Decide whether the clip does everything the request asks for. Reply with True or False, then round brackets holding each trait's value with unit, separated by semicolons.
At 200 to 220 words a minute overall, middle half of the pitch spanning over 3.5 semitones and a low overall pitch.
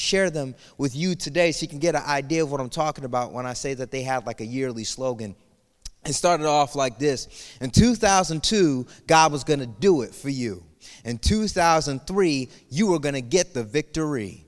False (205 wpm; 4.1 semitones; 145 Hz)